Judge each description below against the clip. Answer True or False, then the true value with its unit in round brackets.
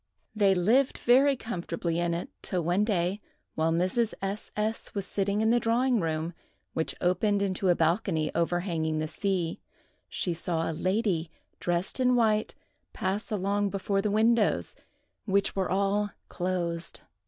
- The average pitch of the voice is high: True (195 Hz)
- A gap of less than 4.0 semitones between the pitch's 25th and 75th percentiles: True (3.6 semitones)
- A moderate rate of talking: True (150 wpm)